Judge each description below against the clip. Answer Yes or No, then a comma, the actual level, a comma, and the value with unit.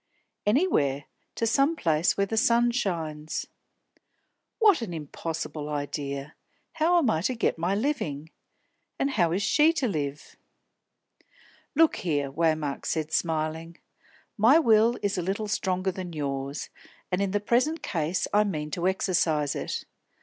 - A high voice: No, medium, 180 Hz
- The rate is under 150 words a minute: Yes, average, 140 wpm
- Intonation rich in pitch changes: Yes, wide, 6.8 semitones